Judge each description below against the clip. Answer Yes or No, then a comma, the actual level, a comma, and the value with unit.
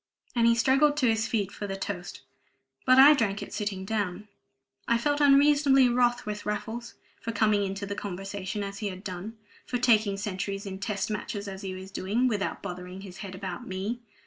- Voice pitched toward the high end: Yes, high, 205 Hz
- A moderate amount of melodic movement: Yes, average, 3.3 semitones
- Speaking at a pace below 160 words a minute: No, average, 195 wpm